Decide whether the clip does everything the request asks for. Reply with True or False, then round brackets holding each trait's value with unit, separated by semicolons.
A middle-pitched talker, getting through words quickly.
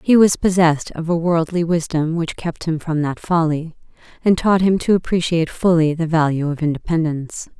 False (165 Hz; 180 wpm)